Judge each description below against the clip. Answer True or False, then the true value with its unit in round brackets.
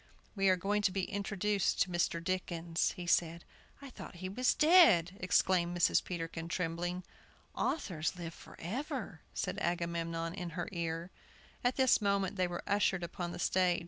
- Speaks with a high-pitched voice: False (180 Hz)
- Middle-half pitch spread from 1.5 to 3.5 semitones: True (2.7 semitones)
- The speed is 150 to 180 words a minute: True (160 wpm)